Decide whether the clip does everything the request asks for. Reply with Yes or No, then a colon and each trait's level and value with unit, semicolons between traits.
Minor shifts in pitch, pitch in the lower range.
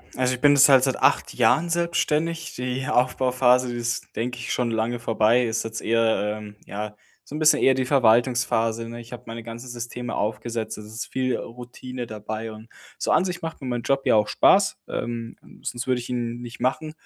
Yes: narrow, 2.2 semitones; low, 120 Hz